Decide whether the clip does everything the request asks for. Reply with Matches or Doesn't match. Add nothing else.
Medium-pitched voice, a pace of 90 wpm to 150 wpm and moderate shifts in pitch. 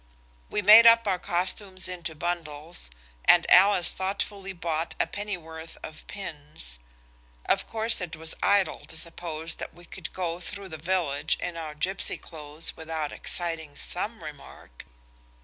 Matches